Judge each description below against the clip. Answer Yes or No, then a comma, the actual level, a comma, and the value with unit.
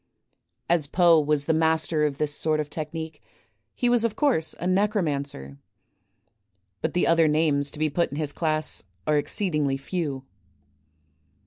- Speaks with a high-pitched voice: No, medium, 155 Hz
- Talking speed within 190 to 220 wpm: No, average, 150 wpm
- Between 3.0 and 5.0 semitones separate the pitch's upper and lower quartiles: No, narrow, 2.5 semitones